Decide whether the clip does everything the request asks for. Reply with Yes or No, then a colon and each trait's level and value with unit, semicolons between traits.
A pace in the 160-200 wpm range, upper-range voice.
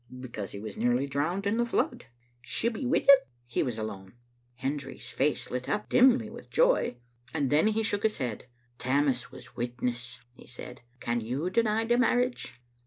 No: average, 190 wpm; low, 135 Hz